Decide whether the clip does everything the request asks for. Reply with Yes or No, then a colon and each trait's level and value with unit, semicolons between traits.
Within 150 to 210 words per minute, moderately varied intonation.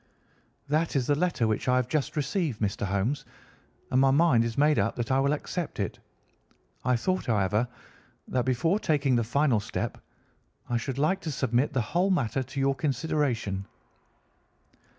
Yes: average, 170 wpm; average, 4.2 semitones